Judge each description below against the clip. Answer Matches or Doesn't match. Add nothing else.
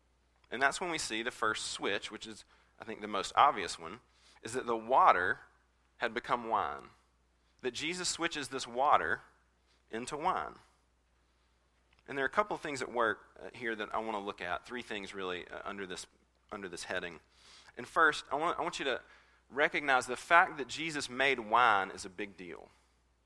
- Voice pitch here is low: Matches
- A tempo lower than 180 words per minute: Doesn't match